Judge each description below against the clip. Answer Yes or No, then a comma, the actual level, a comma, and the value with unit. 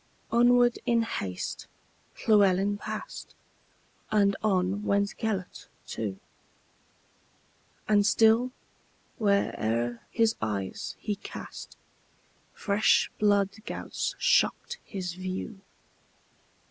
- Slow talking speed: Yes, slow, 70 wpm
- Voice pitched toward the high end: Yes, high, 200 Hz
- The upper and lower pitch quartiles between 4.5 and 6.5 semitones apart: No, average, 3.1 semitones